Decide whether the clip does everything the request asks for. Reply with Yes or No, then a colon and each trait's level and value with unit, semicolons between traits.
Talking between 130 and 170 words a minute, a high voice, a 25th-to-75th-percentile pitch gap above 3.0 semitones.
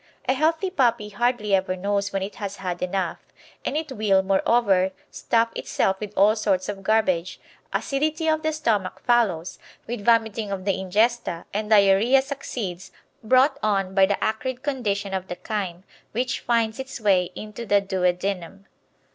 Yes: average, 160 wpm; high, 205 Hz; average, 3.9 semitones